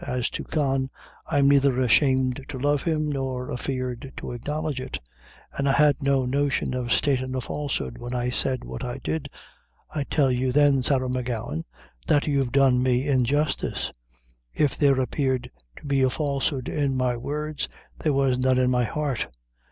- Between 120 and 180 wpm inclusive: Yes, average, 170 wpm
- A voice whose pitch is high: No, low, 135 Hz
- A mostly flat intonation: Yes, narrow, 2.1 semitones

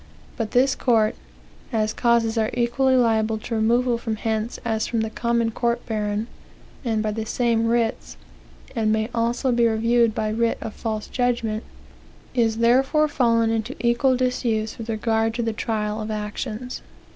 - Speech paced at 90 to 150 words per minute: No, average, 160 wpm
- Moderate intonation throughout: No, narrow, 1.5 semitones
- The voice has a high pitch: Yes, high, 230 Hz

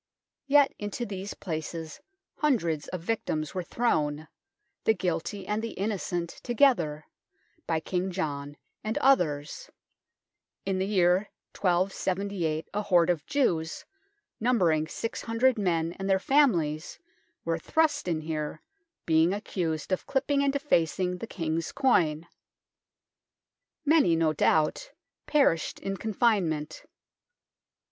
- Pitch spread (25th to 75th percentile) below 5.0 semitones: No, wide, 5.6 semitones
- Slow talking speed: Yes, slow, 115 wpm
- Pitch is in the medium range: Yes, medium, 180 Hz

